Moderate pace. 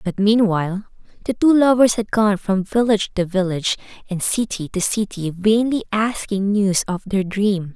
Yes: average, 165 wpm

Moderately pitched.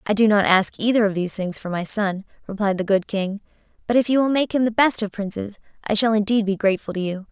No: high, 210 Hz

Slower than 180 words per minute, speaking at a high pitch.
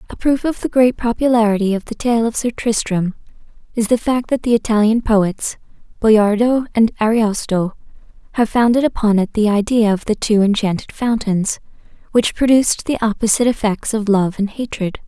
Yes: average, 165 wpm; high, 220 Hz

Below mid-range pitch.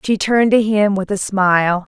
No: high, 200 Hz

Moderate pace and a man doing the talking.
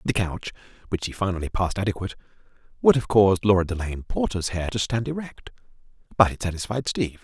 Yes: average, 175 wpm; male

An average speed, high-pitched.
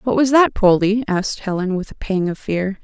No: fast, 235 wpm; high, 205 Hz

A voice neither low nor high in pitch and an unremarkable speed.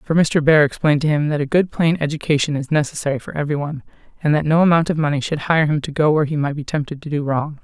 No: medium, 150 Hz; fast, 265 wpm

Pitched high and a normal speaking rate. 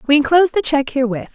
No: very high, 290 Hz; fast, 225 wpm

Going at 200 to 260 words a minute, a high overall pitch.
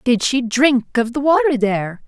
Yes: fast, 205 wpm; very high, 250 Hz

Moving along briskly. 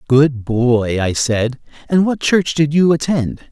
No: average, 170 wpm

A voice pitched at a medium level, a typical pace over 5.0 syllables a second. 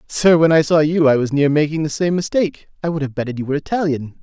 Yes: medium, 155 Hz; 6.6 syllables/s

